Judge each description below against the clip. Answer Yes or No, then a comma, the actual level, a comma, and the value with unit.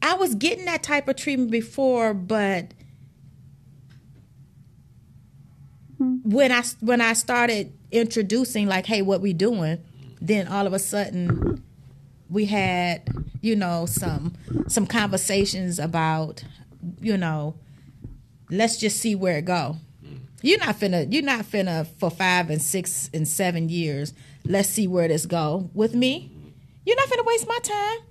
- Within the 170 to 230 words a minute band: No, average, 145 wpm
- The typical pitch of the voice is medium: Yes, medium, 180 Hz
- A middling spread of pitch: No, wide, 7.5 semitones